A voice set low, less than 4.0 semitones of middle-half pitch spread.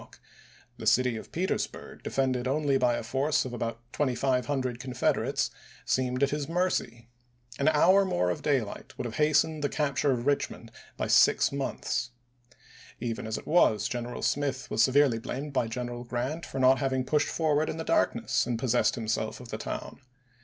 Yes: low, 130 Hz; average, 3.2 semitones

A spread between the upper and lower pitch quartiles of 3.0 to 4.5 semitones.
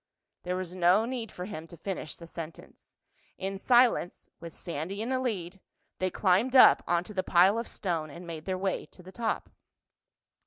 Yes: average, 3.6 semitones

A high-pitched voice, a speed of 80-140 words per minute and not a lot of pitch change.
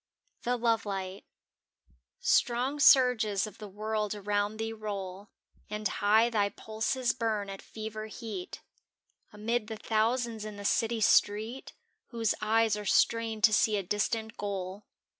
Yes: high, 215 Hz; slow, 135 wpm; narrow, 1.7 semitones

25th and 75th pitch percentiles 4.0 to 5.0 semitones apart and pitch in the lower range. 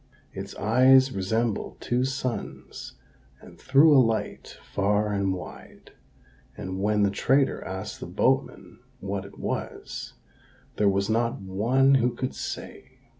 Yes: average, 4.6 semitones; low, 105 Hz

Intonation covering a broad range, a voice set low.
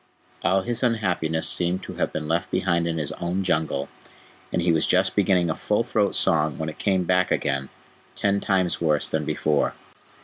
No: average, 3.3 semitones; very low, 85 Hz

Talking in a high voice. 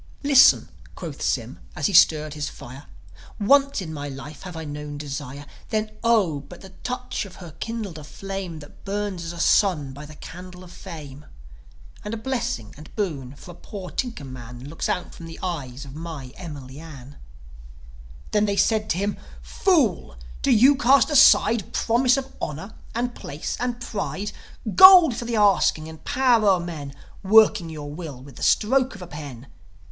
No: medium, 180 Hz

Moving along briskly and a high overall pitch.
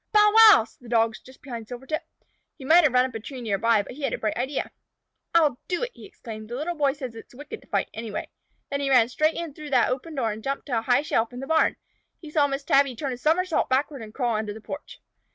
Yes: fast, 270 wpm; very high, 265 Hz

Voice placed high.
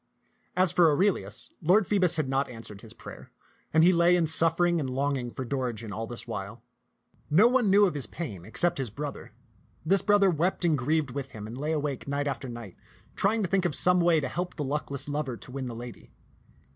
No: medium, 150 Hz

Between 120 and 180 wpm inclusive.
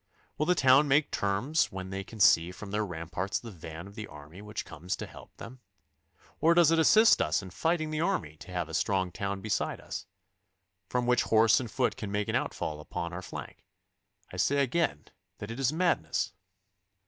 No: average, 200 wpm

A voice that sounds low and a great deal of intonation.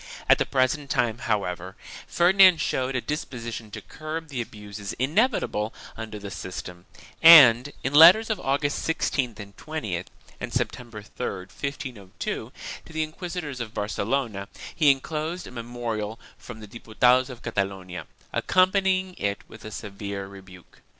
Yes: low, 120 Hz; wide, 6.7 semitones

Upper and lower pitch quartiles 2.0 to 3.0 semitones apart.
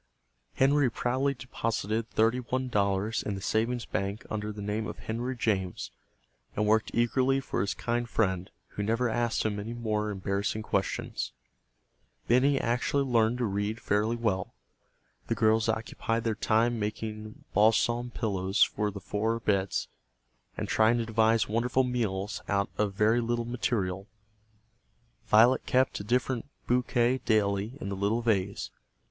Yes: narrow, 2.6 semitones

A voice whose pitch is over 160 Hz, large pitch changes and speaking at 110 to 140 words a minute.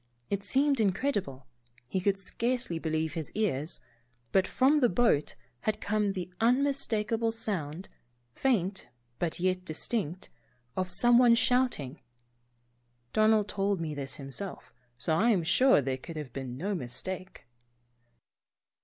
Yes: high, 190 Hz; wide, 6.3 semitones; slow, 135 wpm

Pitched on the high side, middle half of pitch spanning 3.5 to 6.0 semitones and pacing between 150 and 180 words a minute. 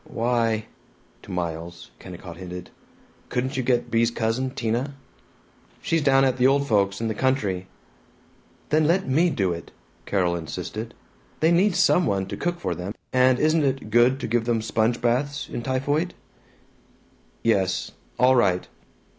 No: low, 120 Hz; average, 5.2 semitones; average, 155 wpm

